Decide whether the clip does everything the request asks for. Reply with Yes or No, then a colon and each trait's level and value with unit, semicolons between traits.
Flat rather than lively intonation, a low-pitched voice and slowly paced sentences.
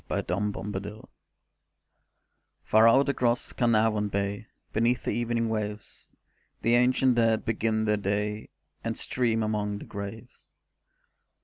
Yes: narrow, 2.1 semitones; low, 110 Hz; slow, 120 wpm